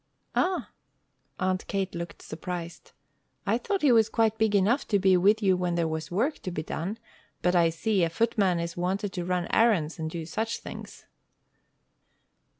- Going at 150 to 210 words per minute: Yes, average, 175 wpm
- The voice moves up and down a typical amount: Yes, average, 4.3 semitones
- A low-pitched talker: No, medium, 185 Hz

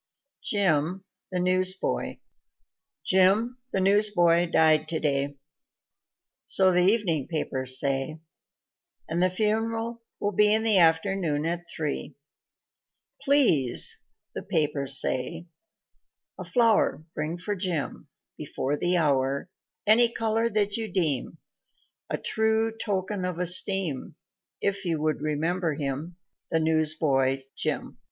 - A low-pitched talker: No, medium, 175 Hz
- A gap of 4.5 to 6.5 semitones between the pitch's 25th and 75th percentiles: Yes, average, 5.0 semitones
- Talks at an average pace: No, slow, 115 wpm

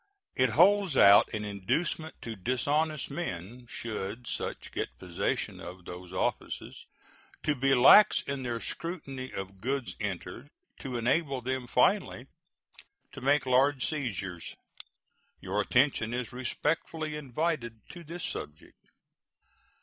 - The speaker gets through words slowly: Yes, slow, 120 wpm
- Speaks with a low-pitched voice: Yes, low, 130 Hz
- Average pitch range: No, wide, 5.9 semitones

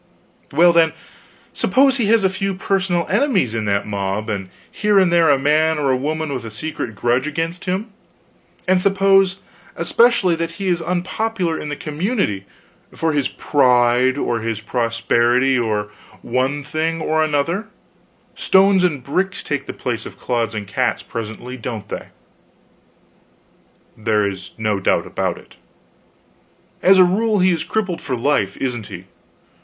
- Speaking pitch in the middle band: Yes, medium, 150 Hz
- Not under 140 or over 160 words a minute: Yes, average, 155 wpm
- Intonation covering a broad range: Yes, wide, 7.7 semitones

